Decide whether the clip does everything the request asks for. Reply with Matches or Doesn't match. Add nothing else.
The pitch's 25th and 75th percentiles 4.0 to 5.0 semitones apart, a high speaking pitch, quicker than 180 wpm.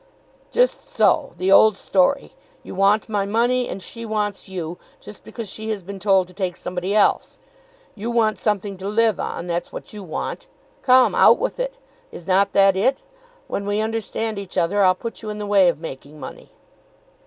Doesn't match